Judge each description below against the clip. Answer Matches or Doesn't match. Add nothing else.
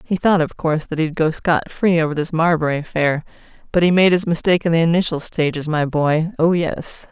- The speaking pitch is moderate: Matches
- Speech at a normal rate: Doesn't match